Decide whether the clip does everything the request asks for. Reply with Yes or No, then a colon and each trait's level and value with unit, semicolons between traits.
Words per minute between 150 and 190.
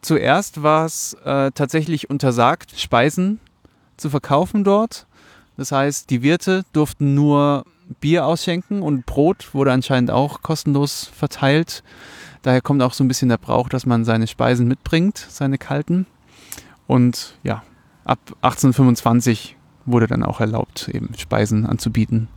No: average, 135 wpm